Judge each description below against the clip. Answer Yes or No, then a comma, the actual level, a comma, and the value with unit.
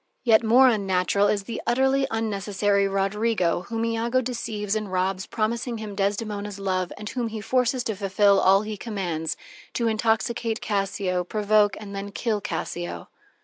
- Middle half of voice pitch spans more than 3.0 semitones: No, narrow, 2.6 semitones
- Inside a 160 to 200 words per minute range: No, average, 150 wpm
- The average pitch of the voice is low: No, high, 210 Hz